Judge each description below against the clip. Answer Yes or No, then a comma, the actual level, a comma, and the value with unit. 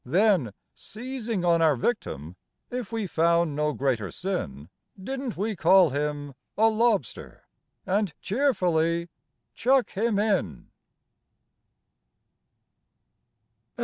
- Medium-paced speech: No, slow, 95 wpm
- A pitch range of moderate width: No, wide, 6.7 semitones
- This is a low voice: No, medium, 185 Hz